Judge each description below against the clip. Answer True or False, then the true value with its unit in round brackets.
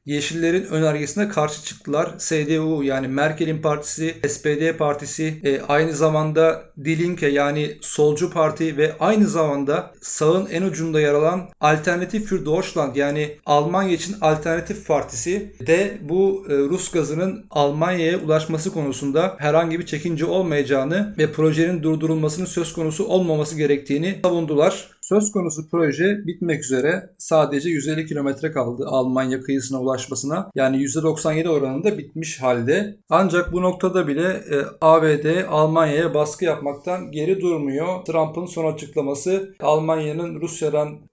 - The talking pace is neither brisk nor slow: True (125 wpm)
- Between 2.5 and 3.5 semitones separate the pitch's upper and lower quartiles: True (2.8 semitones)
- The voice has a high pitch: False (160 Hz)